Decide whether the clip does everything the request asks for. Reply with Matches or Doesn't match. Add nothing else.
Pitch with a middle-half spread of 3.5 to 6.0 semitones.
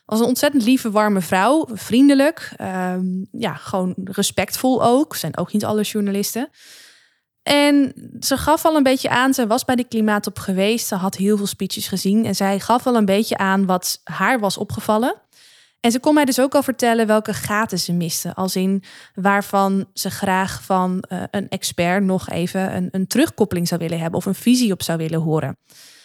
Matches